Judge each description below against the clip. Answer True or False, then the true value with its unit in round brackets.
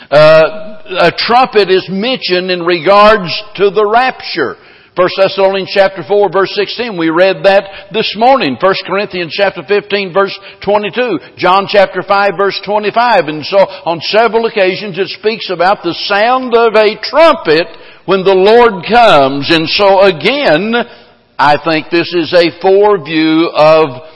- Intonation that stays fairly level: False (3.0 semitones)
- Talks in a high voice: True (195 Hz)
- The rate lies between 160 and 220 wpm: False (145 wpm)